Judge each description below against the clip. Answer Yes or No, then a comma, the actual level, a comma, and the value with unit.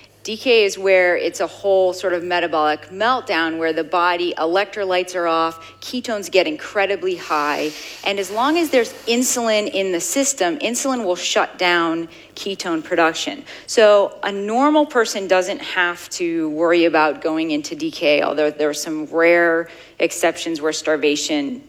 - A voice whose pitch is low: No, medium, 180 Hz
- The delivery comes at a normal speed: Yes, average, 150 wpm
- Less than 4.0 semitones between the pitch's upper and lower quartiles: No, average, 4.7 semitones